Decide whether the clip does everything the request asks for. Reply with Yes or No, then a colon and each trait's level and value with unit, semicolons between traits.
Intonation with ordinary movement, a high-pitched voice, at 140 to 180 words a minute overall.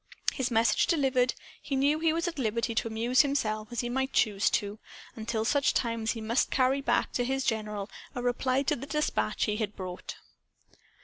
No: average, 3.5 semitones; high, 245 Hz; average, 195 wpm